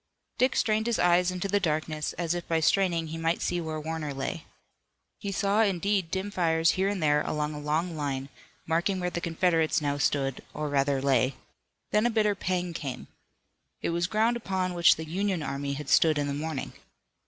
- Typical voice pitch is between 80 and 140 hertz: No, medium, 165 Hz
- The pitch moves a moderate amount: Yes, average, 3.9 semitones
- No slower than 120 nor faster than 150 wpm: No, average, 195 wpm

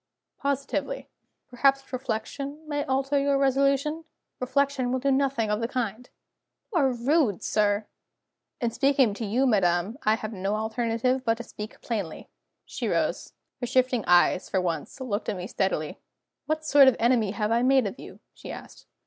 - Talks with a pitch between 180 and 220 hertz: No, high, 245 Hz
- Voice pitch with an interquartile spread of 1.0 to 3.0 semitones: No, average, 4.3 semitones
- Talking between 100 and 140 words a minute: No, average, 165 wpm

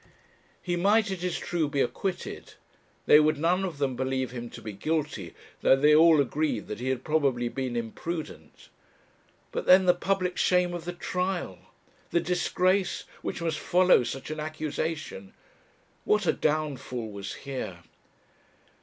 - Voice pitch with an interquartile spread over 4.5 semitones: Yes, average, 5.2 semitones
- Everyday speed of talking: Yes, average, 155 wpm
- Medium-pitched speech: Yes, medium, 155 Hz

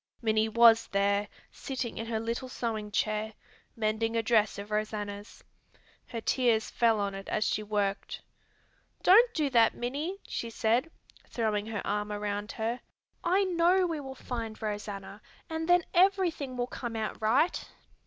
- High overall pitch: Yes, high, 225 Hz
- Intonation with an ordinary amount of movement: Yes, average, 3.7 semitones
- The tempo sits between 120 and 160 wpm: Yes, average, 155 wpm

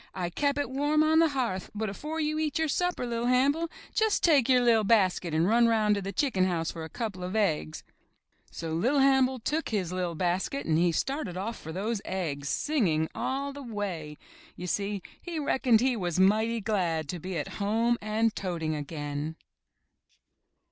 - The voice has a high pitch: Yes, high, 215 Hz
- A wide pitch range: Yes, wide, 7.1 semitones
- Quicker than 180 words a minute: Yes, average, 190 wpm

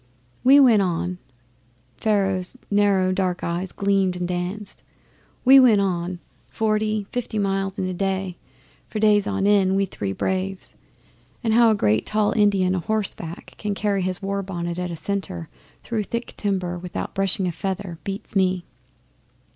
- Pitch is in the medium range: No, high, 195 Hz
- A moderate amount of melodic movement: No, narrow, 2.3 semitones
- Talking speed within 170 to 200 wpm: No, average, 155 wpm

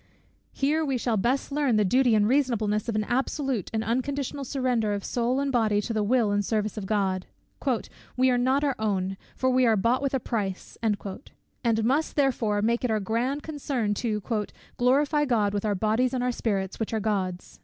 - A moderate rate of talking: Yes, average, 195 wpm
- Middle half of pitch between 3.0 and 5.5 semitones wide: Yes, average, 3.8 semitones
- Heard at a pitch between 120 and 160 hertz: No, high, 230 Hz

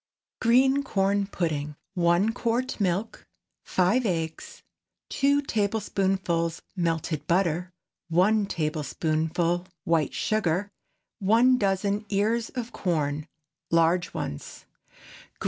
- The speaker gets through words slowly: Yes, slow, 90 wpm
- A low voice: No, medium, 185 Hz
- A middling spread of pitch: Yes, average, 4.6 semitones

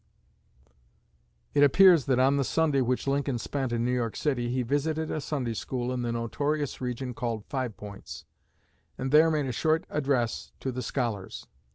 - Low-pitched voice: Yes, low, 130 Hz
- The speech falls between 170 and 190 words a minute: Yes, average, 175 wpm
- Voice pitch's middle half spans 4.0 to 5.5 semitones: No, average, 3.1 semitones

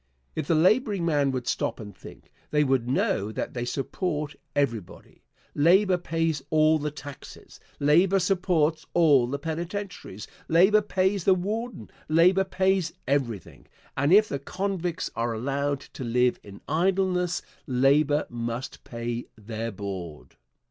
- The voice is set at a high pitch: No, medium, 150 Hz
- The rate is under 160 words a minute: Yes, slow, 135 wpm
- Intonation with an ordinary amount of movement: No, wide, 6.4 semitones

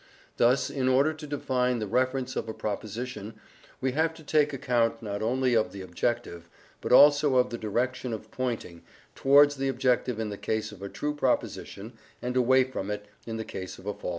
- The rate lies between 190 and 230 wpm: Yes, fast, 205 wpm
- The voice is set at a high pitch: No, low, 125 Hz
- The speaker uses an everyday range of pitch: Yes, average, 3.4 semitones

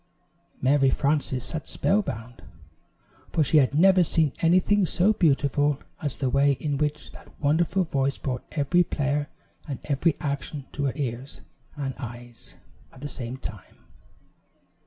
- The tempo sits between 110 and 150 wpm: Yes, average, 140 wpm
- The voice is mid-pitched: Yes, medium, 145 Hz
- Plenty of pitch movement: No, average, 3.0 semitones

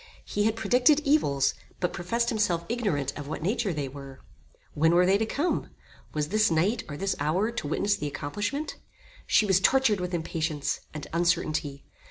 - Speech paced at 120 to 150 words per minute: No, average, 175 wpm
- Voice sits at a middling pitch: Yes, medium, 180 Hz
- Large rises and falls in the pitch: Yes, wide, 6.4 semitones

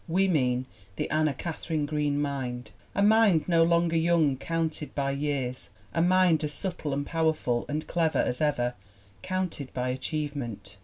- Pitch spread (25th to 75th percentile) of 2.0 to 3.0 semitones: No, average, 3.6 semitones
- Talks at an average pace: Yes, average, 160 wpm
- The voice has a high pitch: No, medium, 150 Hz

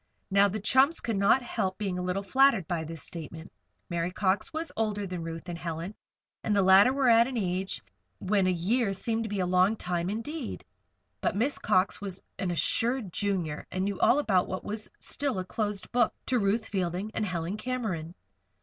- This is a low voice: No, high, 195 Hz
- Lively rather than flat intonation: No, average, 3.7 semitones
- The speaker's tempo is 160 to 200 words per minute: Yes, average, 195 wpm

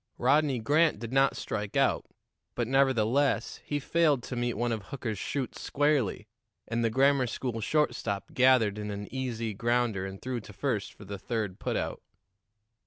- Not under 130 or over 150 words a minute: No, average, 170 wpm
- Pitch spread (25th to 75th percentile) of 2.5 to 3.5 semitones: No, average, 4.2 semitones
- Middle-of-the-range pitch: No, low, 120 Hz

